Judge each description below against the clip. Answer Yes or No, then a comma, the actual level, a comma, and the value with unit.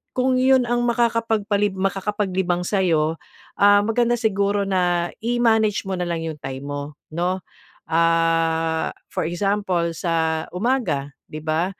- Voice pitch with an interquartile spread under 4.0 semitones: No, average, 4.6 semitones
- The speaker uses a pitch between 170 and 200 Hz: Yes, medium, 185 Hz